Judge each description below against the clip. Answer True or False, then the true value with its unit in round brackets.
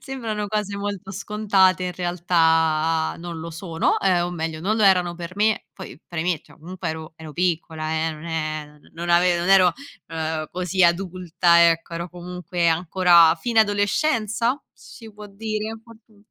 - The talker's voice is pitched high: False (180 Hz)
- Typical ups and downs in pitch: True (3.6 semitones)